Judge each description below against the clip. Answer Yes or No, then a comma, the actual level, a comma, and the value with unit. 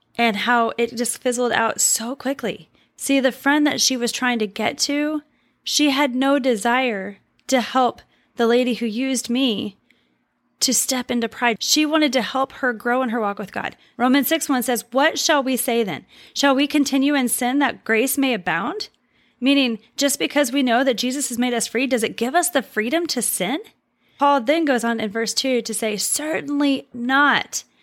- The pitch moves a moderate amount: Yes, average, 3.1 semitones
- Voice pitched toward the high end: Yes, very high, 255 Hz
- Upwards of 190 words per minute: Yes, average, 200 wpm